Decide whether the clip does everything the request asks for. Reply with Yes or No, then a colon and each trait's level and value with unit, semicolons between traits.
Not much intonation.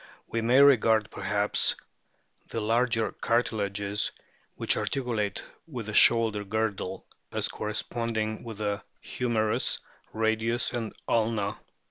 Yes: narrow, 1.7 semitones